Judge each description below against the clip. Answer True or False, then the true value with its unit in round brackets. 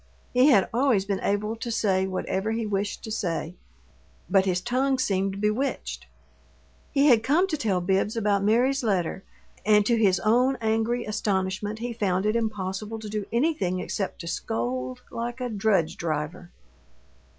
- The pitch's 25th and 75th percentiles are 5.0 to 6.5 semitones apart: False (3.6 semitones)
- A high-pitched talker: True (210 Hz)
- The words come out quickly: False (160 wpm)